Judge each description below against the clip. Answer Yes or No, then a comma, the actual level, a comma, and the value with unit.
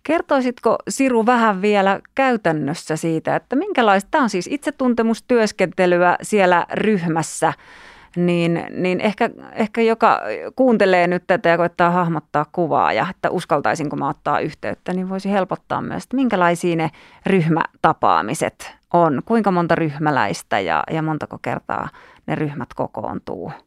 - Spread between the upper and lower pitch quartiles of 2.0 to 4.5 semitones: No, wide, 5.4 semitones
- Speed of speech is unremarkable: Yes, average, 130 wpm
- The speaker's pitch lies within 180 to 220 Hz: Yes, high, 190 Hz